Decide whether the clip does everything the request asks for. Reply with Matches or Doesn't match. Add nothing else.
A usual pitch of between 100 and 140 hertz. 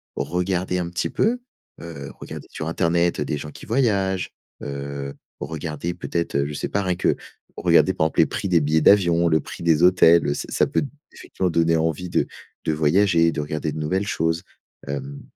Doesn't match